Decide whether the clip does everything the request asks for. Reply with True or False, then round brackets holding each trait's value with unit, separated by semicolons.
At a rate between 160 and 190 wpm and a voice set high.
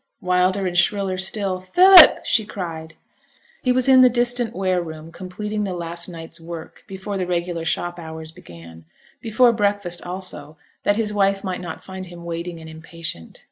False (170 wpm; 180 Hz)